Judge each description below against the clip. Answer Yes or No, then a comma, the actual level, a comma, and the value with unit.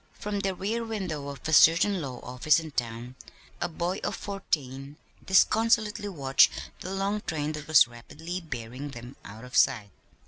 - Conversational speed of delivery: Yes, average, 165 wpm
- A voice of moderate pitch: Yes, medium, 155 Hz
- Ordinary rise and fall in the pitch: No, wide, 6.9 semitones